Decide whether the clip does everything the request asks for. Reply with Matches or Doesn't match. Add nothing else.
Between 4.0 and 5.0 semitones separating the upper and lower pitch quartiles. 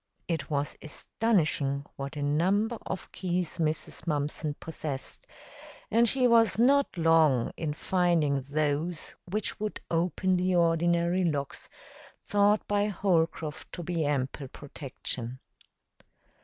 Matches